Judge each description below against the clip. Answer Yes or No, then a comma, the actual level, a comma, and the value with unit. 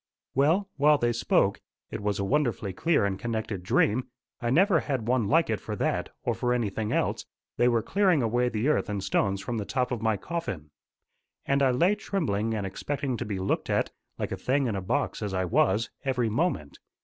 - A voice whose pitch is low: Yes, low, 120 Hz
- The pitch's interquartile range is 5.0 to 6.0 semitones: Yes, wide, 5.6 semitones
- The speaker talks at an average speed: No, fast, 210 wpm